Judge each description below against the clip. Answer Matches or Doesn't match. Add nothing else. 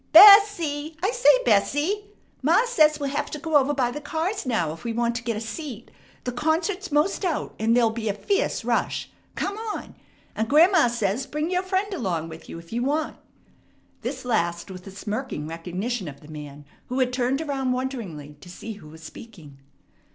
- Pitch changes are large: Matches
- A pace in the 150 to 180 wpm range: Doesn't match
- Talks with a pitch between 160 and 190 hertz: Doesn't match